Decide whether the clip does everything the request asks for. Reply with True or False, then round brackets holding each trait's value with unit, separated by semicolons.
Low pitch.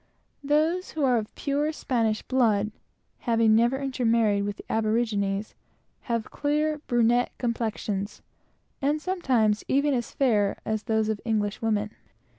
False (230 Hz)